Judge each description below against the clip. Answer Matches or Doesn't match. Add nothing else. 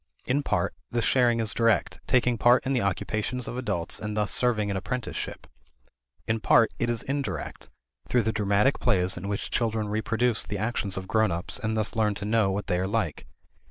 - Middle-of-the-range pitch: Doesn't match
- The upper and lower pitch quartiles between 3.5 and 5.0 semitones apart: Doesn't match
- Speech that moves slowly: Doesn't match